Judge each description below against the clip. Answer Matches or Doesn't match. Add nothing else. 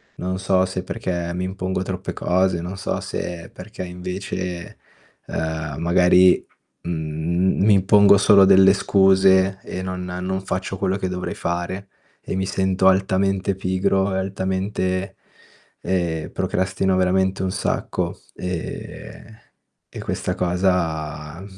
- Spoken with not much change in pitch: Matches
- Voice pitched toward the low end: Matches